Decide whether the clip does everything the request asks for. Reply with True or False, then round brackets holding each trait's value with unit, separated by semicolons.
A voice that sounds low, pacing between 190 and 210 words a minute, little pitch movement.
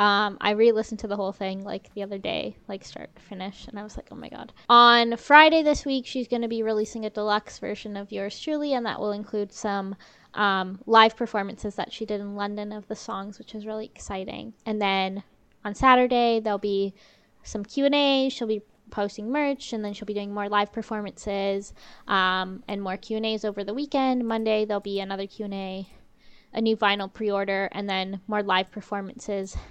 False (210 Hz; 200 wpm; 2.1 semitones)